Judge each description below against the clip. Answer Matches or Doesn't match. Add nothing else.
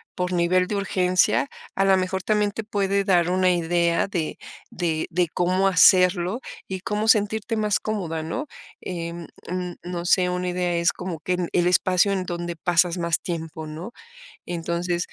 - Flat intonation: Matches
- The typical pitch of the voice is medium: Matches